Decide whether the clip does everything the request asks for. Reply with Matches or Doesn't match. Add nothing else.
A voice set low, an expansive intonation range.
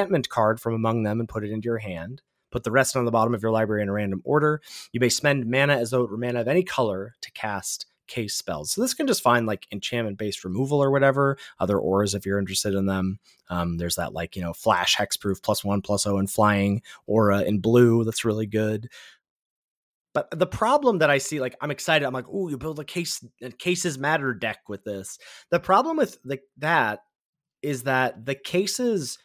Matches